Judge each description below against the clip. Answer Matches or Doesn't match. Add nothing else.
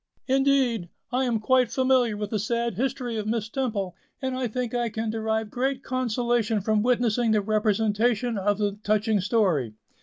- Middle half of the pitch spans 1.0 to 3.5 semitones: Matches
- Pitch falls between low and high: Doesn't match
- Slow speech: Doesn't match